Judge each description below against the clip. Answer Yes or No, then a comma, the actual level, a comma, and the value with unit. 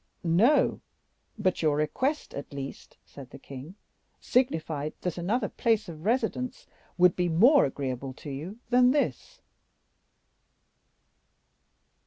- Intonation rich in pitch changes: Yes, wide, 8.5 semitones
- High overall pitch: No, medium, 175 Hz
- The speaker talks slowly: Yes, slow, 115 wpm